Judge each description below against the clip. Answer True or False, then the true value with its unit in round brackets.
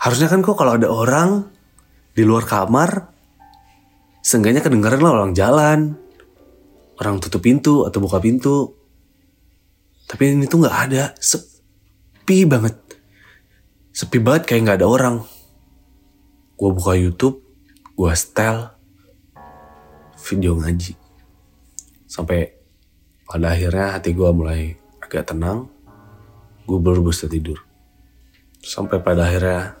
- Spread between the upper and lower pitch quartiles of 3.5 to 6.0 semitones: True (5.2 semitones)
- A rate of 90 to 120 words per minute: True (110 wpm)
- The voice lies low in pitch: True (95 Hz)